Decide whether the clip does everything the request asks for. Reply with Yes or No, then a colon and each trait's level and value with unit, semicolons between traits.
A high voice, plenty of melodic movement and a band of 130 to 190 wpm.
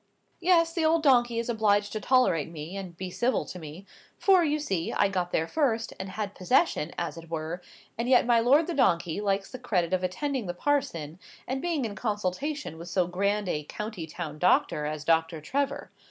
No: high, 200 Hz; wide, 7.1 semitones; average, 200 wpm